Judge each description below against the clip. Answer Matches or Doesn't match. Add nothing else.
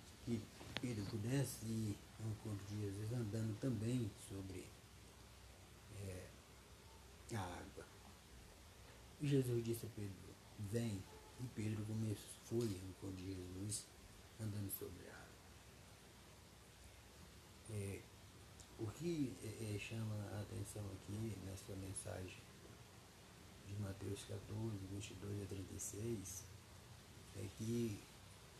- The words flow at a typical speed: Doesn't match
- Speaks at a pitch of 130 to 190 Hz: Doesn't match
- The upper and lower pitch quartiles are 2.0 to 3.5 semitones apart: Matches